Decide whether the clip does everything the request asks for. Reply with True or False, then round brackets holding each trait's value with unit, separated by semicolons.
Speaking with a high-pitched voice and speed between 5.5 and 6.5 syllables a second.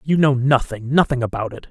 False (130 Hz; 5.7 syllables/s)